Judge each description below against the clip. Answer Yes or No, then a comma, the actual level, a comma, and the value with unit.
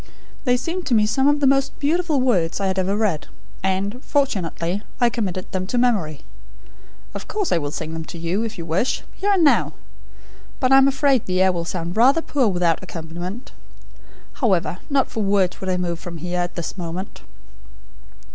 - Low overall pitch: No, high, 195 Hz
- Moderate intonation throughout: No, wide, 6.9 semitones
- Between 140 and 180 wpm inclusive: No, average, 195 wpm